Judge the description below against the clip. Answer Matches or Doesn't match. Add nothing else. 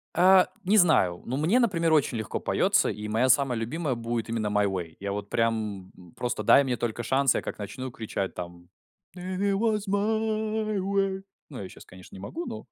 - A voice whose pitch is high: Doesn't match